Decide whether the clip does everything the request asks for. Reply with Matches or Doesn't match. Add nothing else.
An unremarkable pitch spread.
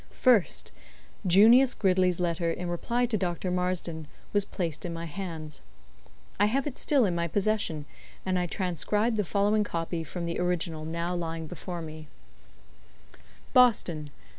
Matches